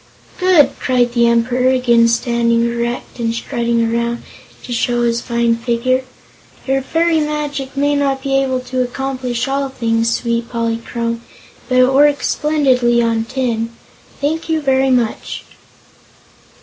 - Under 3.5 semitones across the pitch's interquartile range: Yes, narrow, 2.4 semitones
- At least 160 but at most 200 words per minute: No, slow, 135 wpm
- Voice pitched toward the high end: Yes, very high, 250 Hz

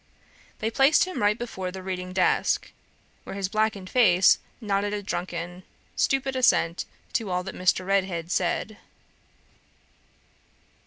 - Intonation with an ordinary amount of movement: Yes, average, 3.1 semitones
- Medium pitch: No, high, 195 Hz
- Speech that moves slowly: Yes, slow, 125 wpm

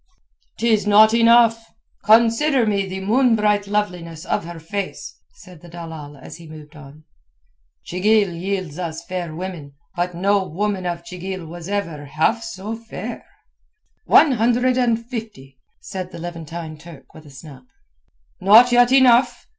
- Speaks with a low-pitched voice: No, high, 190 Hz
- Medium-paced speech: Yes, average, 145 wpm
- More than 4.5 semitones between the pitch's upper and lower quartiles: Yes, average, 5.1 semitones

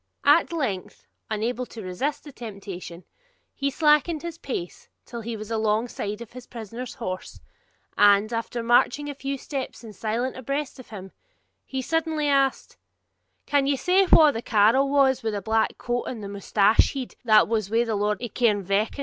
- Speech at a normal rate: Yes, average, 175 wpm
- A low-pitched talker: No, high, 235 Hz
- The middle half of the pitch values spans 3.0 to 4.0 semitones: No, average, 4.4 semitones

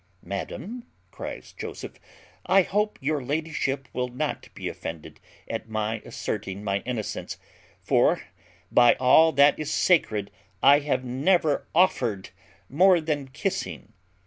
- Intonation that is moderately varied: No, wide, 6.3 semitones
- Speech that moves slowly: Yes, slow, 120 wpm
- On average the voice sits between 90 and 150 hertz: Yes, medium, 140 Hz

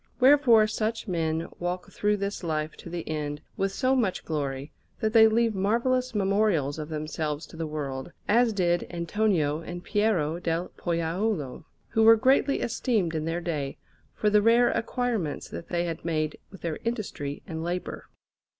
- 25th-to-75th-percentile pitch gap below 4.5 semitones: No, wide, 5.6 semitones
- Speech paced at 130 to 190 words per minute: Yes, average, 165 wpm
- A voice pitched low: No, medium, 175 Hz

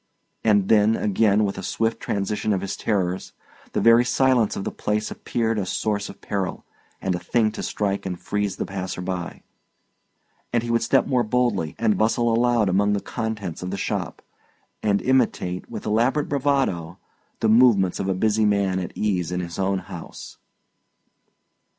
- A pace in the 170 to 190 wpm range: Yes, average, 175 wpm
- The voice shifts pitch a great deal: No, average, 3.2 semitones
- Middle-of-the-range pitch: No, low, 105 Hz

